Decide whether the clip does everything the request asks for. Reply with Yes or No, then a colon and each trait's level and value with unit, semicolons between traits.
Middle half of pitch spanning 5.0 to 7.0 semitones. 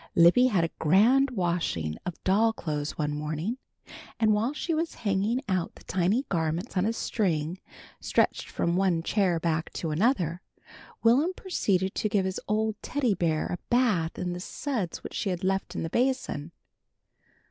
Yes: average, 5.3 semitones